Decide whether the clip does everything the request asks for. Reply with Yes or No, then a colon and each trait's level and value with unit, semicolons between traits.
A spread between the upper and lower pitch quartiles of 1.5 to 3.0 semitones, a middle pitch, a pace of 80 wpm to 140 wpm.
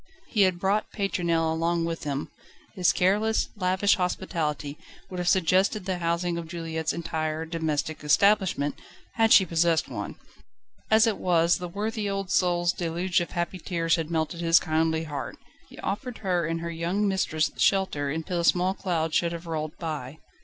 No: narrow, 2.6 semitones; medium, 170 Hz; average, 165 wpm